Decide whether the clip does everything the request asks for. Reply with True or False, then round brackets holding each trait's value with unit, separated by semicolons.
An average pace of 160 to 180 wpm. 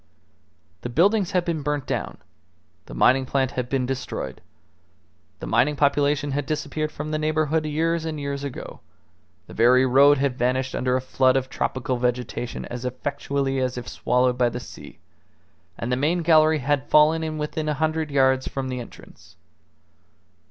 True (165 wpm)